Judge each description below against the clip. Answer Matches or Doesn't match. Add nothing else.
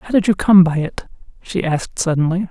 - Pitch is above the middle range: Doesn't match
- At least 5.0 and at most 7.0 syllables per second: Matches